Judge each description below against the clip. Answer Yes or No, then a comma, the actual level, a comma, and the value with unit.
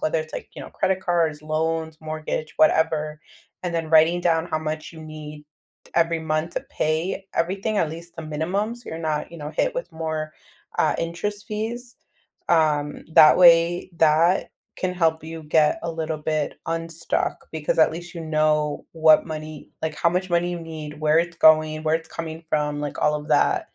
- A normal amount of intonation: No, narrow, 1.6 semitones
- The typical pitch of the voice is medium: Yes, medium, 160 Hz